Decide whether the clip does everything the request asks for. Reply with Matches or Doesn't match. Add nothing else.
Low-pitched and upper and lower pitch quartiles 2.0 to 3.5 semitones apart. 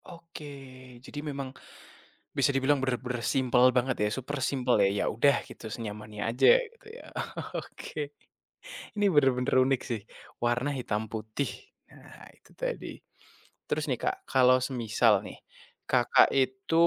Matches